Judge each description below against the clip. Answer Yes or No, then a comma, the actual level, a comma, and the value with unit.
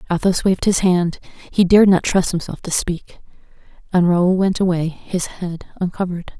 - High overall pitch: No, medium, 180 Hz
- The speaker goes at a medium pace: Yes, average, 160 wpm